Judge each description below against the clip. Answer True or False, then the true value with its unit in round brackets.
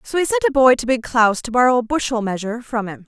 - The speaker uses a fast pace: True (290 wpm)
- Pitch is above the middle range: True (245 Hz)